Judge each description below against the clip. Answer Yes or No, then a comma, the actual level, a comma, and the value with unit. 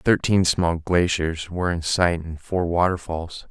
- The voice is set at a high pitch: No, very low, 85 Hz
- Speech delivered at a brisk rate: No, average, 155 wpm